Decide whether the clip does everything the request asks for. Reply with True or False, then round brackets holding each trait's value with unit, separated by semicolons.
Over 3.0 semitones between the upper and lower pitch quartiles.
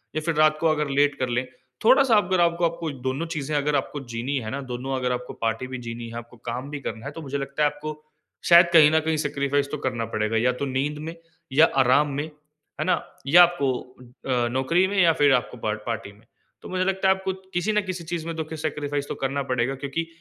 True (4.2 semitones)